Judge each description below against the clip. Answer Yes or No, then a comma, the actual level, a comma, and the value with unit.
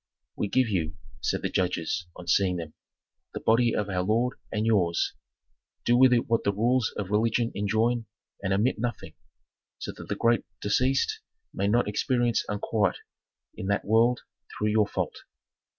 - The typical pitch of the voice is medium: No, low, 110 Hz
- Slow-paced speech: No, average, 165 wpm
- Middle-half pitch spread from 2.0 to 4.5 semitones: Yes, average, 3.2 semitones